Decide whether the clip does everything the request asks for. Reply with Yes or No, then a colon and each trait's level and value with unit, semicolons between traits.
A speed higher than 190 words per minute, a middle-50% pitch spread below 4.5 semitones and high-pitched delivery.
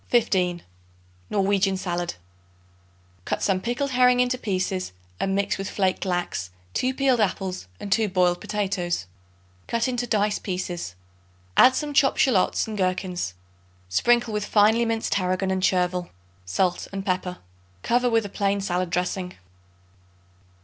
No: slow, 135 wpm; average, 3.8 semitones; high, 195 Hz